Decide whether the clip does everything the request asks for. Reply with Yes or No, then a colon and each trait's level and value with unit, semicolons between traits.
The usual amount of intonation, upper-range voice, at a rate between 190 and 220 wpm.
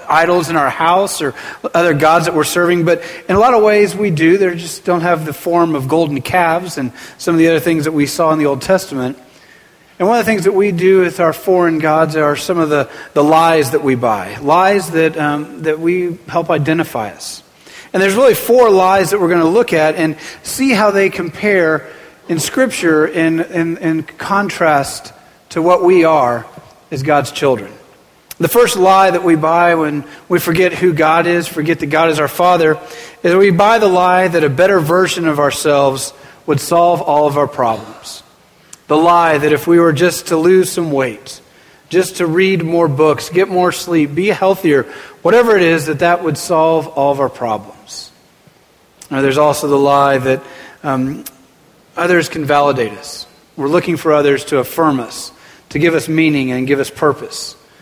No: average, 3.2 semitones; medium, 165 Hz; average, 200 wpm